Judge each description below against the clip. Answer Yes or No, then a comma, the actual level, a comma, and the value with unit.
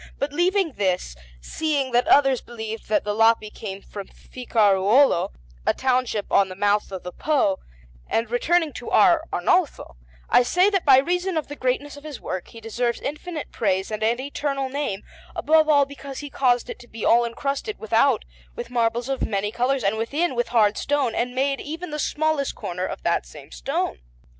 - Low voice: No, very high, 250 Hz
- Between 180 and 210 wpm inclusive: Yes, average, 185 wpm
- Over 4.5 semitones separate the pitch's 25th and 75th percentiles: Yes, average, 5.0 semitones